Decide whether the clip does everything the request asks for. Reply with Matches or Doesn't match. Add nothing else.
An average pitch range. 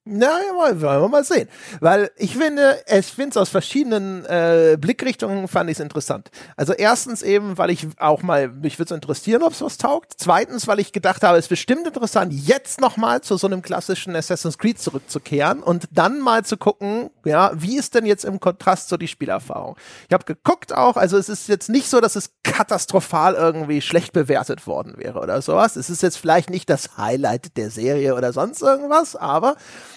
Doesn't match